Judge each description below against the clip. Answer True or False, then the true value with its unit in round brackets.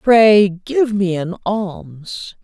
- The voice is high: False (180 Hz)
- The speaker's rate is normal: False (125 wpm)